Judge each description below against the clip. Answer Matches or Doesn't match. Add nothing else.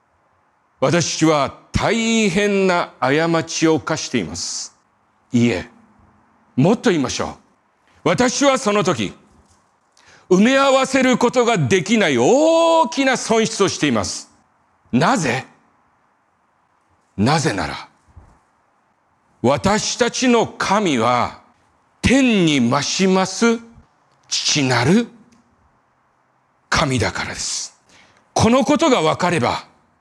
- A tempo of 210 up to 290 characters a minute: Doesn't match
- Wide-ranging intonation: Matches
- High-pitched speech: Matches